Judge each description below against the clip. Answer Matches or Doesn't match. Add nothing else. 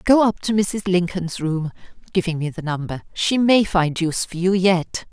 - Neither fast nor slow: Matches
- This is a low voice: Doesn't match